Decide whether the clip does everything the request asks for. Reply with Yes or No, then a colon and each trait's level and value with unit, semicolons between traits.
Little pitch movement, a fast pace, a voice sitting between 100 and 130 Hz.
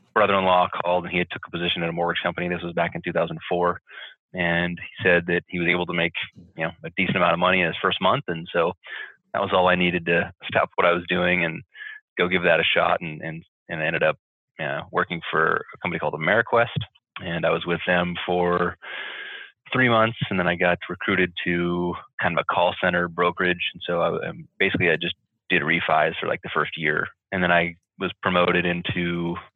No: narrow, 1.0 semitones; fast, 220 wpm; very low, 90 Hz